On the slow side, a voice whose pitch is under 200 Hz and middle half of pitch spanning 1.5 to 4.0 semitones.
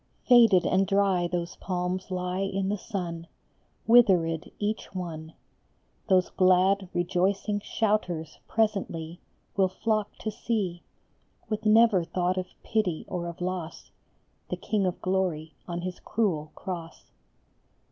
Yes: slow, 125 wpm; medium, 185 Hz; average, 2.7 semitones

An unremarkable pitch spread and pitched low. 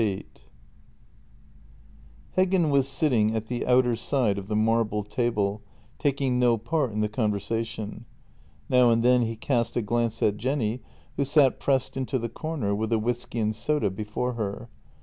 Yes: average, 3.3 semitones; low, 115 Hz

